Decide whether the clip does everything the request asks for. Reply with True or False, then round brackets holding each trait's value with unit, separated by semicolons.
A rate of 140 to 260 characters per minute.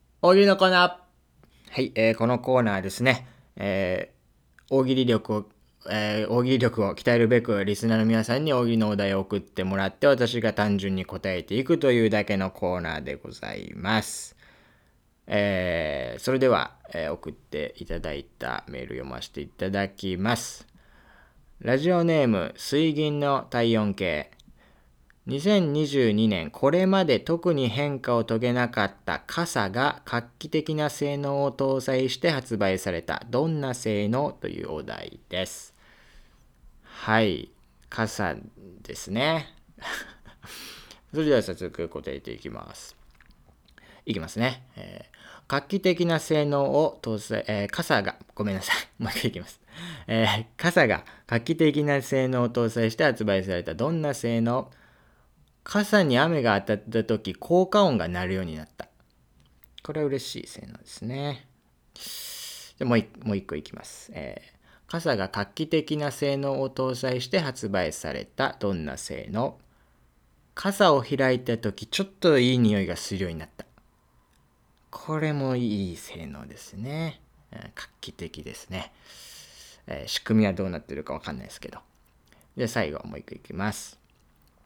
False (275 characters per minute)